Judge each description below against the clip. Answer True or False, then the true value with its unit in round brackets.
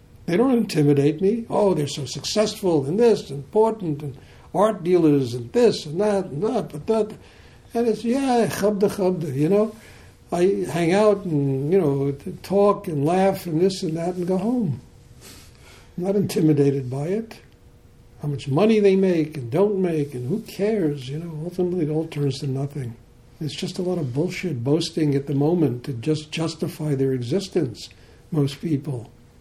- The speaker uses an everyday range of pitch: False (5.7 semitones)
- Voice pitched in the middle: True (165 Hz)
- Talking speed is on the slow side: False (175 wpm)